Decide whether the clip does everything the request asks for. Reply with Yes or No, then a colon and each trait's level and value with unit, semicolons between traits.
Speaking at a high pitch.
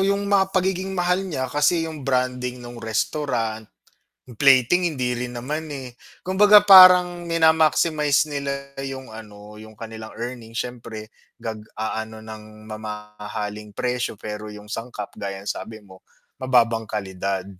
No: low, 125 Hz